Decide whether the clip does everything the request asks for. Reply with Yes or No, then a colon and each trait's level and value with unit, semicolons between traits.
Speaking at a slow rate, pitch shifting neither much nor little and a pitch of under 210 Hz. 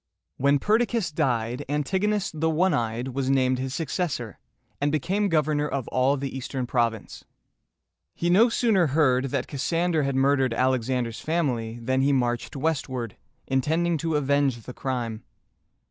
No: average, 150 wpm; average, 4.1 semitones; low, 135 Hz